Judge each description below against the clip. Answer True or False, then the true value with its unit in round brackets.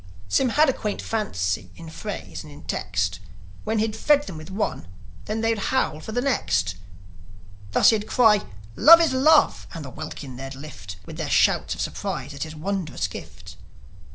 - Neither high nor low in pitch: False (195 Hz)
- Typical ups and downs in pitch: False (9.0 semitones)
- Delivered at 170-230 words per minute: True (180 wpm)